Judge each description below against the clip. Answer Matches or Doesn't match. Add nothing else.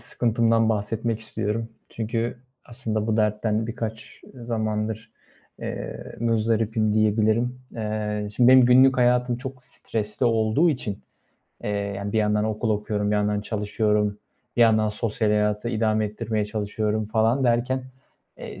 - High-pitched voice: Doesn't match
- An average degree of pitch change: Doesn't match